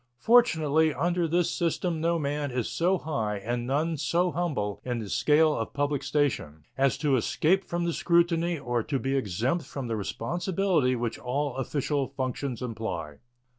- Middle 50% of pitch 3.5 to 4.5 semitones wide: No, wide, 5.5 semitones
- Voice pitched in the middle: Yes, medium, 145 Hz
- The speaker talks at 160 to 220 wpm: Yes, average, 165 wpm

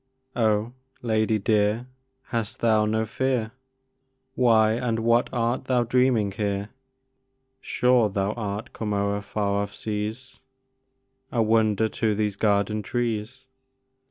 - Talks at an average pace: No, slow, 120 wpm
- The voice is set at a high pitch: No, low, 110 Hz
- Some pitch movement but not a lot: No, narrow, 2.1 semitones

